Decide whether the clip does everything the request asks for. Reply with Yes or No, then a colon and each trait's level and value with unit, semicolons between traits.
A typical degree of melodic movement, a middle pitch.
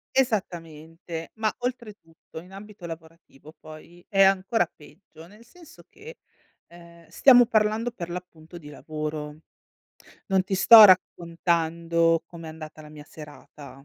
Yes: average, 4.2 semitones; medium, 170 Hz